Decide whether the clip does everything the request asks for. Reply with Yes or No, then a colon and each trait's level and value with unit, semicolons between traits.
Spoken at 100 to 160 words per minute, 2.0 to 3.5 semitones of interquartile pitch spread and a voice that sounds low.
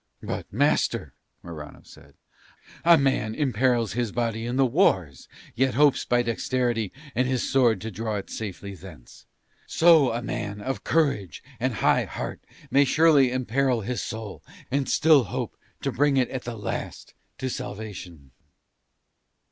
No: average, 150 wpm; average, 4.2 semitones; low, 120 Hz